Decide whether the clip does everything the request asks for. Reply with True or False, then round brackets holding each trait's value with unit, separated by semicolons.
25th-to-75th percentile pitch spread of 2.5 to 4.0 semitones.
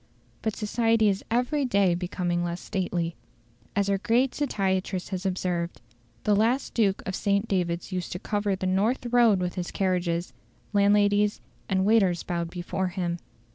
True (2.9 semitones)